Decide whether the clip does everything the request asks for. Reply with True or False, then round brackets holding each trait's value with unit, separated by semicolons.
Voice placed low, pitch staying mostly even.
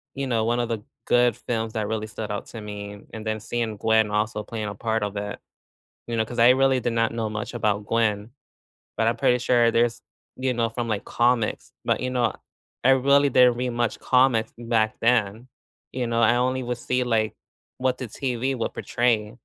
True (115 Hz; 2.2 semitones)